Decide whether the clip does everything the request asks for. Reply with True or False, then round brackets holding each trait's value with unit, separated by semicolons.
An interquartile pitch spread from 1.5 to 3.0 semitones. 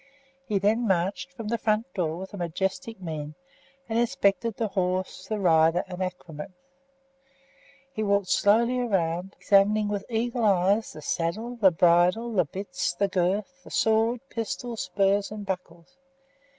False (3.8 semitones)